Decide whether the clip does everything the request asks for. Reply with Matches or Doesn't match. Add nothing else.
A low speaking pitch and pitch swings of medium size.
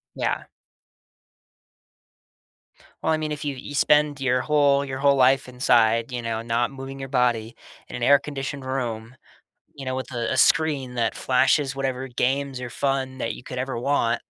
Doesn't match